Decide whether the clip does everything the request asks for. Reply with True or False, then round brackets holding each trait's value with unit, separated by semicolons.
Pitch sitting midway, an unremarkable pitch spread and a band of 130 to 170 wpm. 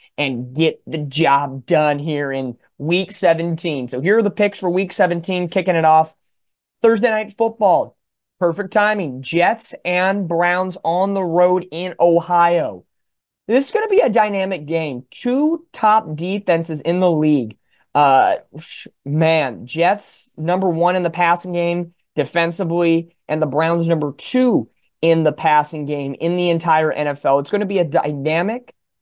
True (170 Hz; 3.4 semitones; 155 wpm)